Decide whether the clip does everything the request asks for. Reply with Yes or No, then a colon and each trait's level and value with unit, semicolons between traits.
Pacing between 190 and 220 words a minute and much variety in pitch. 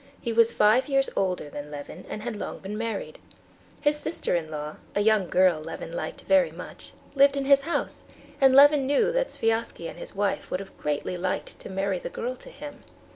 Yes: fast, 205 wpm; wide, 7.0 semitones